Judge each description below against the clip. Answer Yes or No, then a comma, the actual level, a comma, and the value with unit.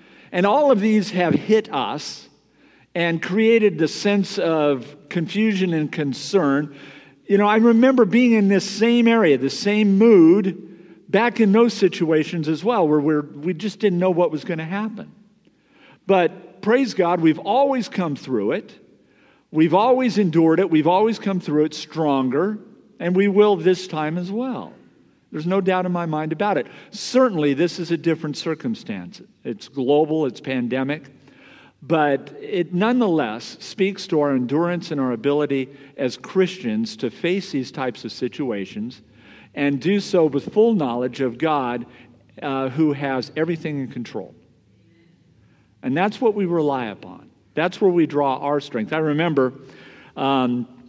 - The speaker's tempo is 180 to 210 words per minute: No, average, 160 wpm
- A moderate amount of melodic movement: No, wide, 6.1 semitones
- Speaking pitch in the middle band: Yes, medium, 170 Hz